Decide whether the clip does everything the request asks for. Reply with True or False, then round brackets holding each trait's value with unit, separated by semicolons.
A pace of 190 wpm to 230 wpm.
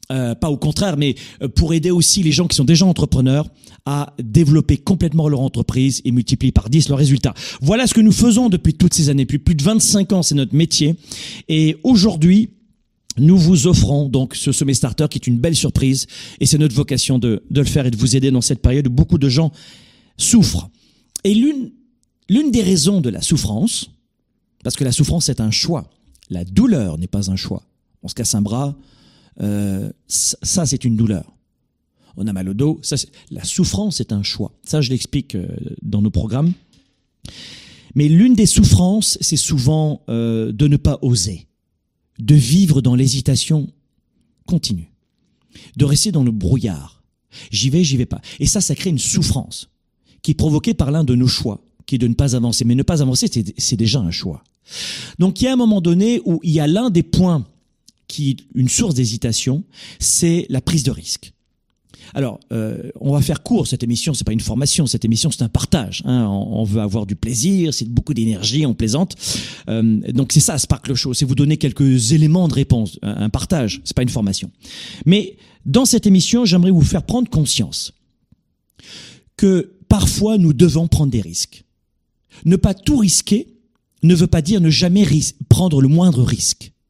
True (195 wpm)